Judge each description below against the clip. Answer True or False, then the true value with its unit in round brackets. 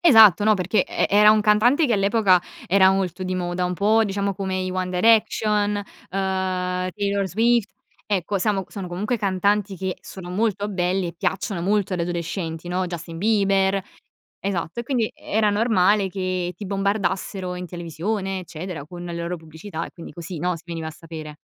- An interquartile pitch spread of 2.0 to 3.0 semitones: True (2.7 semitones)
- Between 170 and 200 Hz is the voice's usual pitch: True (190 Hz)